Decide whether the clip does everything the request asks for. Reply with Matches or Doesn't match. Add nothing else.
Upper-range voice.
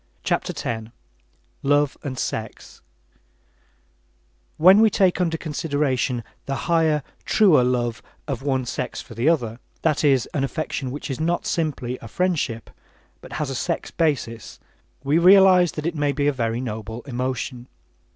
Doesn't match